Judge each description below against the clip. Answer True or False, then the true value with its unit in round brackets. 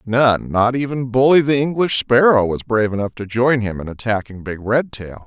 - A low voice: True (115 Hz)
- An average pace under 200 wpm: False (205 wpm)